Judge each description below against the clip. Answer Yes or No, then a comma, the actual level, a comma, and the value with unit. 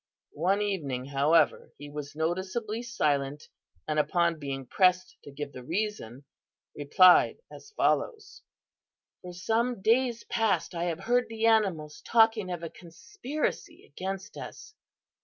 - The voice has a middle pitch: Yes, medium, 180 Hz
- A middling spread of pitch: No, wide, 6.8 semitones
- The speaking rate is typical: No, slow, 130 wpm